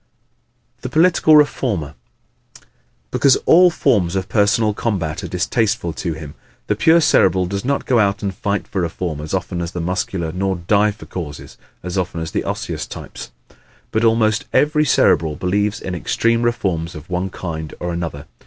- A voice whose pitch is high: No, very low, 95 Hz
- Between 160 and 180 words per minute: Yes, average, 170 wpm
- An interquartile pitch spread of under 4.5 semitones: No, average, 4.8 semitones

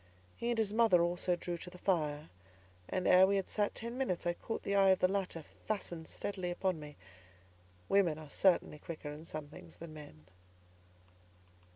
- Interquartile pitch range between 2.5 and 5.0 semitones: Yes, average, 3.8 semitones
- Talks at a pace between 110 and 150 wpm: No, average, 185 wpm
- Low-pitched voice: No, medium, 180 Hz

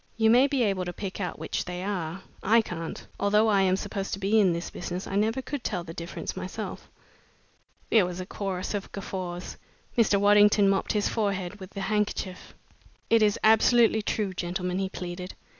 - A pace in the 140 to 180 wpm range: No, average, 190 wpm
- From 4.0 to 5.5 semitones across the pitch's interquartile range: No, average, 2.7 semitones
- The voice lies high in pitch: Yes, high, 195 Hz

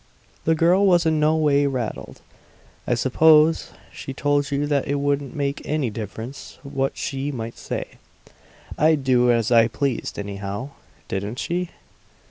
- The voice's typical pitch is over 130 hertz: Yes, medium, 140 Hz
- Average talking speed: Yes, average, 145 wpm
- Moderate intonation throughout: Yes, average, 3.9 semitones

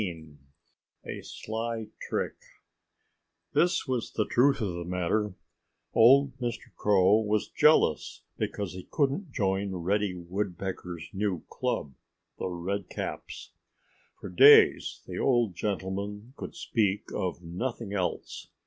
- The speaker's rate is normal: No, slow, 115 wpm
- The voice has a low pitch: Yes, low, 100 Hz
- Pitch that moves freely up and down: No, average, 4.1 semitones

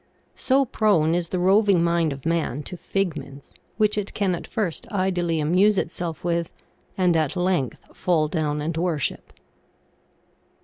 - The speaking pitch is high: No, medium, 175 Hz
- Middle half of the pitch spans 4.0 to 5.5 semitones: No, average, 3.1 semitones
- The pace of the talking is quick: No, average, 150 wpm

